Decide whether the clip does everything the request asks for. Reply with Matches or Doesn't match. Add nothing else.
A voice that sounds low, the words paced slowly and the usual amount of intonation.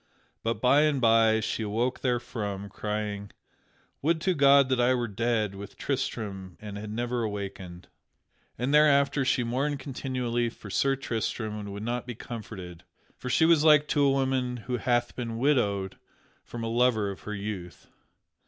Doesn't match